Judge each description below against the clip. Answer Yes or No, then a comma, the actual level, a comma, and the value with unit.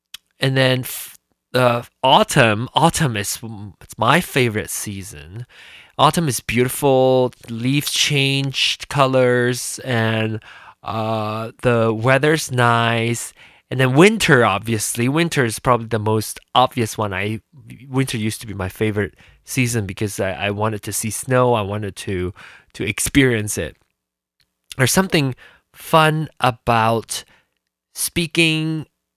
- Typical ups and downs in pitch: Yes, average, 3.9 semitones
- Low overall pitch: Yes, low, 120 Hz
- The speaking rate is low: Yes, slow, 125 wpm